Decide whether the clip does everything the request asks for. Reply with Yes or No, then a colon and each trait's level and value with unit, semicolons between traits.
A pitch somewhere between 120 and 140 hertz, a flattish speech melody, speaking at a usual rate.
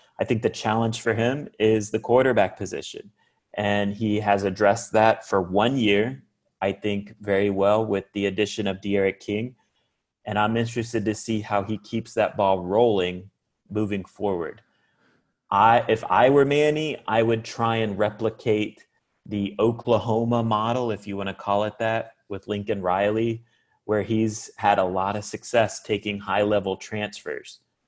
No: low, 105 Hz; narrow, 2.0 semitones; average, 160 wpm